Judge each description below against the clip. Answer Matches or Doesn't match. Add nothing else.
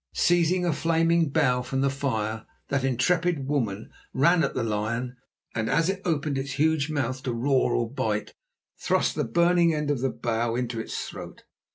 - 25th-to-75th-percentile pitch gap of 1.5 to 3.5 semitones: Doesn't match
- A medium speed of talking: Matches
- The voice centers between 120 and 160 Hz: Matches